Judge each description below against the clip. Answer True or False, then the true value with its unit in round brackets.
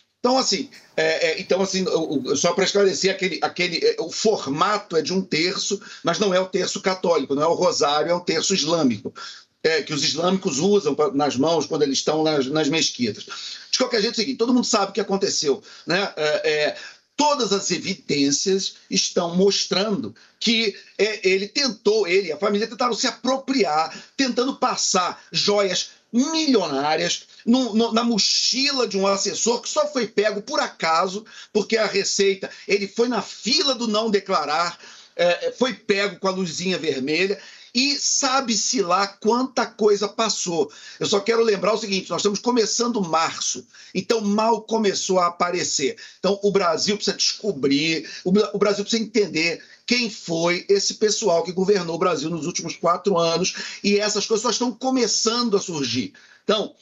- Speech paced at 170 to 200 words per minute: True (175 wpm)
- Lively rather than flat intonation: False (4.4 semitones)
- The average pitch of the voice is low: False (200 Hz)